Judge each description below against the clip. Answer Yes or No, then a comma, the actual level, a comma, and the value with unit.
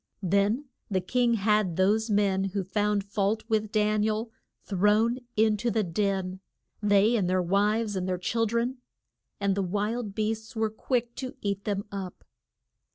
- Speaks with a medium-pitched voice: No, high, 210 Hz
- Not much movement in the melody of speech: Yes, narrow, 2.1 semitones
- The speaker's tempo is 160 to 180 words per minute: Yes, average, 165 wpm